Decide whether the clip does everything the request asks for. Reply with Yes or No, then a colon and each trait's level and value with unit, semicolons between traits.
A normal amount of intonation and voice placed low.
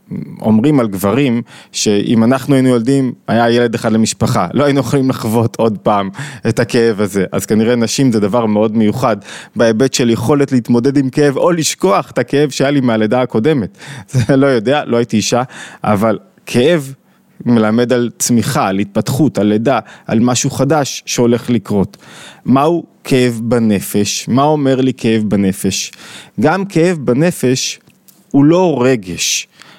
Yes: average, 3.9 semitones; low, 120 Hz